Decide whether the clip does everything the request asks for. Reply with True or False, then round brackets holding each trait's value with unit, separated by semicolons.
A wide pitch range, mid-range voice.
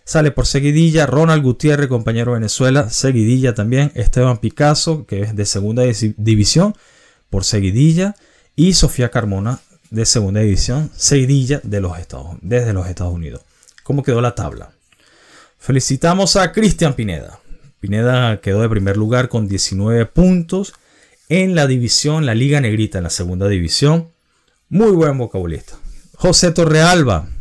False (6.8 semitones; 125 Hz)